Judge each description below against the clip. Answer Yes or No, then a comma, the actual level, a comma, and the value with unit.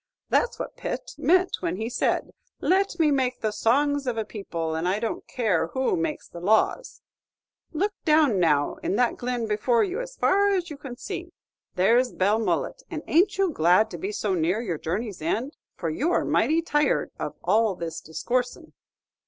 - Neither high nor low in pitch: No, high, 240 Hz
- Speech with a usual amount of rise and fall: No, wide, 8.6 semitones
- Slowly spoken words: No, average, 180 wpm